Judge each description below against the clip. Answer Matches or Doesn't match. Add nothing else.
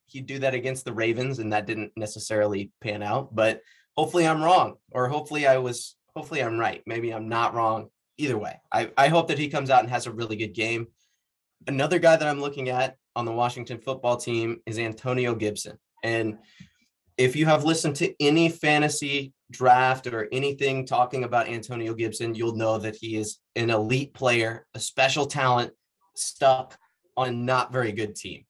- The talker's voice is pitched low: Matches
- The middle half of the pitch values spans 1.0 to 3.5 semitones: Matches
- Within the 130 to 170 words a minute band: Doesn't match